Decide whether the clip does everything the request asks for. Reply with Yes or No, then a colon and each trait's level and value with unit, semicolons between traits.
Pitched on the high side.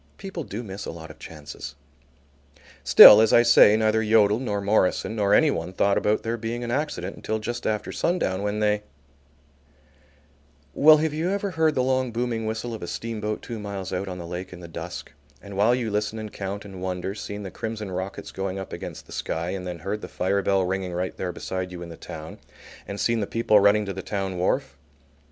No: low, 105 Hz